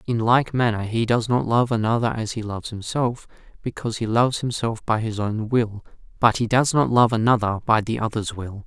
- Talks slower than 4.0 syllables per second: No, 5.4 syllables/s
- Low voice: Yes, low, 115 Hz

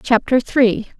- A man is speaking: No, female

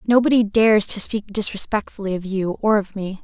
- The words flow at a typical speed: Yes, average, 185 wpm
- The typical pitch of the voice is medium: No, high, 205 Hz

